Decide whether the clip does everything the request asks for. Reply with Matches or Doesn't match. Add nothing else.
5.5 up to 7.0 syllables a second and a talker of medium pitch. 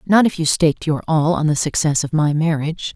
Matches